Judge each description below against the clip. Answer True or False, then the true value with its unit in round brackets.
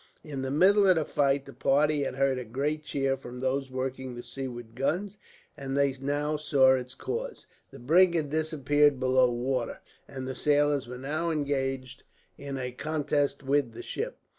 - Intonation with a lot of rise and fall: False (2.4 semitones)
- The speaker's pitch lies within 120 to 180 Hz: True (135 Hz)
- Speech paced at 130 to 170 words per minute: False (185 wpm)